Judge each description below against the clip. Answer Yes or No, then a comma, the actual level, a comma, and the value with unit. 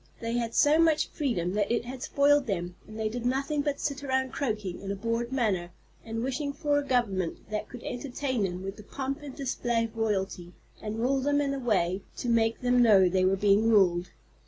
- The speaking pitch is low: No, high, 230 Hz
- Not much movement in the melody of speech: No, average, 5.1 semitones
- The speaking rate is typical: No, fast, 215 wpm